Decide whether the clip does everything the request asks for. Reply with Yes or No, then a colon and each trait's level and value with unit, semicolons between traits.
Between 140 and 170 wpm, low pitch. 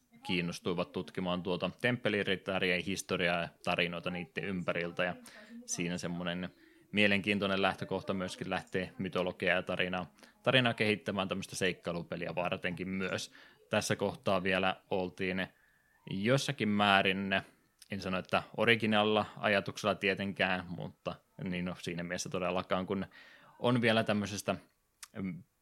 No: average, 110 wpm; very low, 95 Hz